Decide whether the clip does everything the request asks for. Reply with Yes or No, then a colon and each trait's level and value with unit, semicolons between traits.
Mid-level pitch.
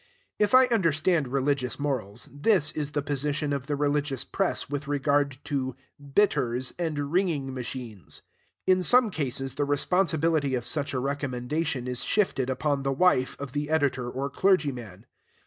Yes: medium, 145 Hz